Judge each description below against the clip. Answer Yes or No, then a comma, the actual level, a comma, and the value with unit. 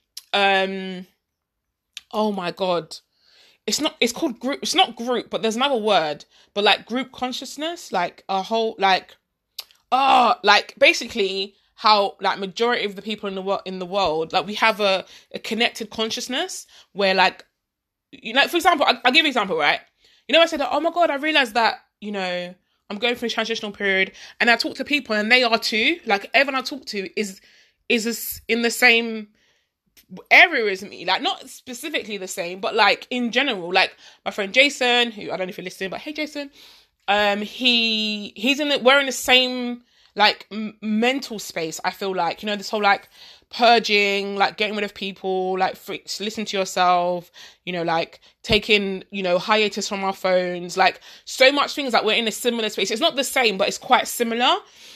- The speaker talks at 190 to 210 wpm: Yes, average, 200 wpm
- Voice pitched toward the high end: Yes, high, 215 Hz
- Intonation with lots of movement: No, average, 4.3 semitones